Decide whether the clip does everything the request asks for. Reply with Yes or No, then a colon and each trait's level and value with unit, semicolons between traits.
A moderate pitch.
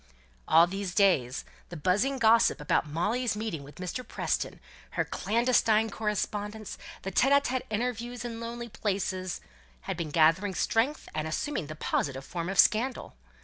No: high, 210 Hz